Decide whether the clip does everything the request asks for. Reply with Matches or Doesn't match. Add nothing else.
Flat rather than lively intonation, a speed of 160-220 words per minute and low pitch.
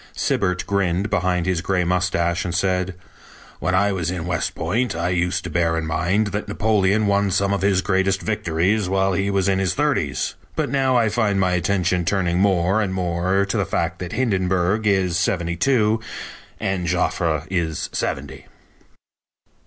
Matches